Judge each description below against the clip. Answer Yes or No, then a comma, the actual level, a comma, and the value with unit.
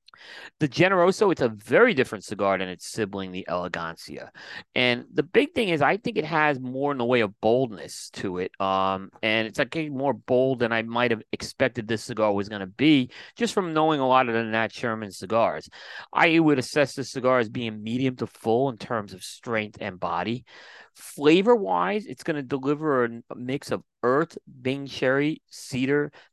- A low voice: Yes, low, 125 Hz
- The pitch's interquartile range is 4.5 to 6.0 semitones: Yes, average, 4.8 semitones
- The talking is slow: No, average, 195 wpm